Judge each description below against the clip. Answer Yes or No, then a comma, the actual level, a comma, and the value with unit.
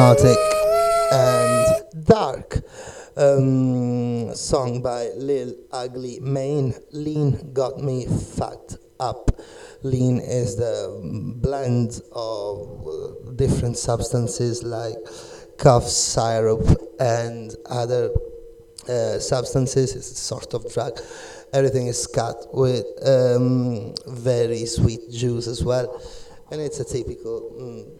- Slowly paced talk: Yes, slow, 100 wpm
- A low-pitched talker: Yes, low, 125 Hz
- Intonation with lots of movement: No, average, 3.8 semitones